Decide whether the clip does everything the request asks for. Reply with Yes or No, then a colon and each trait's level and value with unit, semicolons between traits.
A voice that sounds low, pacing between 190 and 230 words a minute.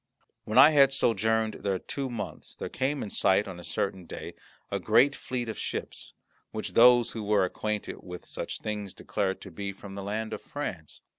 Yes: low, 105 Hz; average, 195 wpm